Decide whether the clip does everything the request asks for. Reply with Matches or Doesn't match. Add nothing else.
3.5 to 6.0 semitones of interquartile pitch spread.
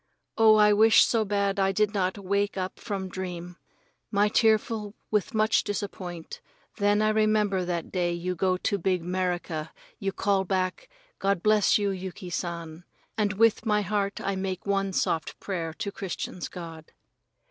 Doesn't match